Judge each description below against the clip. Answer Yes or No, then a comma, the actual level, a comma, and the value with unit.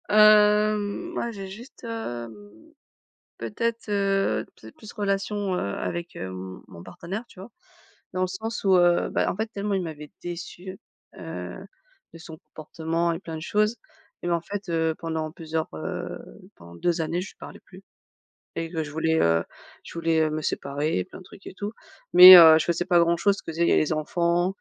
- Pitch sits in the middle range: Yes, medium, 170 Hz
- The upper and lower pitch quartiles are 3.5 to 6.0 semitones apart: Yes, average, 3.8 semitones